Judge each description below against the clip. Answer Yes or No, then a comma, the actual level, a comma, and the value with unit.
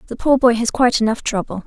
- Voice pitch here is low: No, high, 230 Hz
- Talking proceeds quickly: Yes, fast, 250 wpm